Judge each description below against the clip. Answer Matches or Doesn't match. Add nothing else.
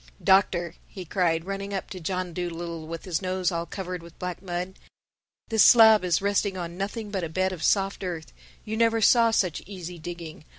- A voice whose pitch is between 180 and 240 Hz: Matches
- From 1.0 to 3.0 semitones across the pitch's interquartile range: Matches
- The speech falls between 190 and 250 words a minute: Matches